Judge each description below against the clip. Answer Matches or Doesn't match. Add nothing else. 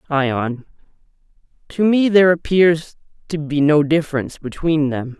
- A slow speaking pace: Matches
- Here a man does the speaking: Matches